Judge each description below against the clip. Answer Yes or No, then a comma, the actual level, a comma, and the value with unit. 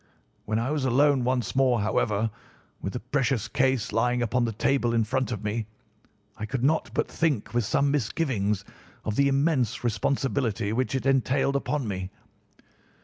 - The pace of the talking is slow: No, average, 165 wpm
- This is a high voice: No, low, 125 Hz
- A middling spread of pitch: Yes, average, 3.7 semitones